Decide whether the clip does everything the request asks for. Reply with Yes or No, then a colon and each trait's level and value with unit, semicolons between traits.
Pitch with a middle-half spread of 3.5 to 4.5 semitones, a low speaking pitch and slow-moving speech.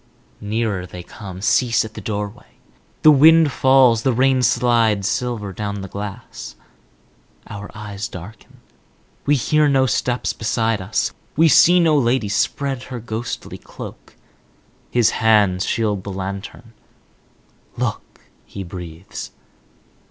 Yes: average, 4.1 semitones; low, 110 Hz; slow, 125 wpm